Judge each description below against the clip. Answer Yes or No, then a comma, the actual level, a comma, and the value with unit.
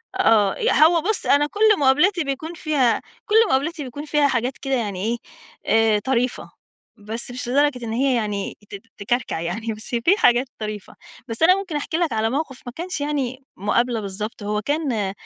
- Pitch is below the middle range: No, very high, 255 Hz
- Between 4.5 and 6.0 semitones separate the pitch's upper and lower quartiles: Yes, average, 5.2 semitones